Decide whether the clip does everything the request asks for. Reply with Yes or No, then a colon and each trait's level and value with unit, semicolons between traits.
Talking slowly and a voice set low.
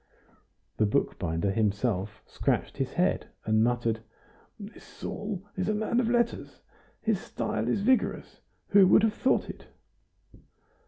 Yes: slow, 130 wpm; low, 130 Hz